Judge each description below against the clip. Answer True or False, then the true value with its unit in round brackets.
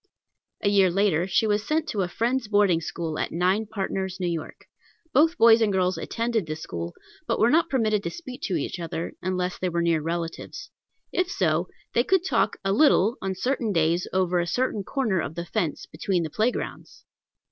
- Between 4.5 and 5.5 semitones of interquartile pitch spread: True (4.8 semitones)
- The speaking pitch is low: False (190 Hz)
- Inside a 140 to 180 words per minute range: False (190 wpm)